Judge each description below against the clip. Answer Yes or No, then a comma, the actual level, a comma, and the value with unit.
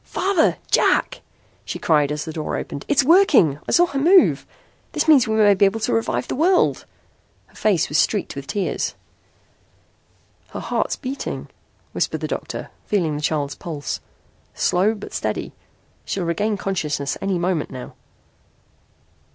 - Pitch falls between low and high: No, high, 195 Hz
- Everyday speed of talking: Yes, average, 150 wpm